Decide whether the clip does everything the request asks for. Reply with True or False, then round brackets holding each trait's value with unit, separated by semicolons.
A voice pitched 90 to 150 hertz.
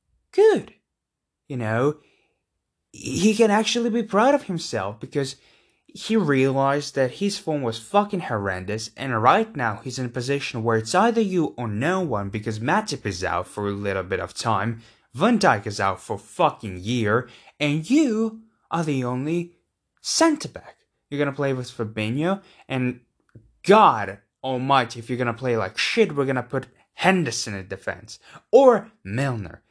True (135 Hz)